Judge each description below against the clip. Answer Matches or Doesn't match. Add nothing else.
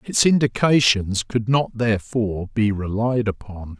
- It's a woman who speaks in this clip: Doesn't match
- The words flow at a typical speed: Doesn't match